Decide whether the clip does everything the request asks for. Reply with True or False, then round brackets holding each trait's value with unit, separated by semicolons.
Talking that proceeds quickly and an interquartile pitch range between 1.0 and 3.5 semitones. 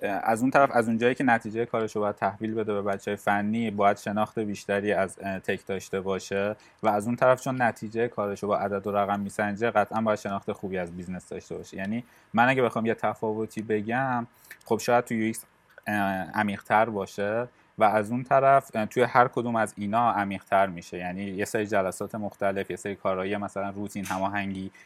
True (190 wpm; 2.4 semitones)